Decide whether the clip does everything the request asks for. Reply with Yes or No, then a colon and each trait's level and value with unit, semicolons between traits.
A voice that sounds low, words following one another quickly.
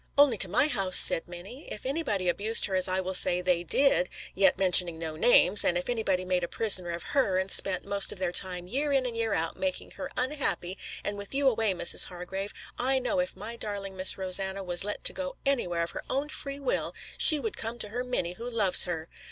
No: high, 195 Hz; fast, 225 wpm